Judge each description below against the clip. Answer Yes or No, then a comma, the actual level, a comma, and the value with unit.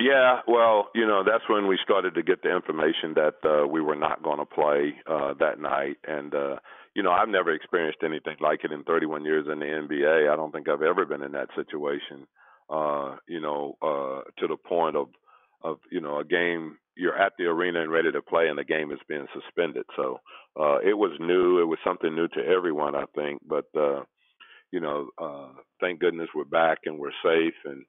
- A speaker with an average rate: No, fast, 215 wpm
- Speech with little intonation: Yes, narrow, 2.2 semitones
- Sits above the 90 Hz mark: No, very low, 75 Hz